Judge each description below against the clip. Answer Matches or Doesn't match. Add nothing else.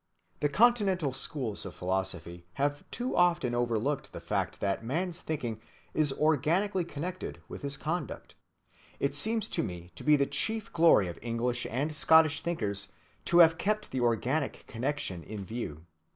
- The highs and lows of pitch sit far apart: Matches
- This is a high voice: Doesn't match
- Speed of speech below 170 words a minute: Matches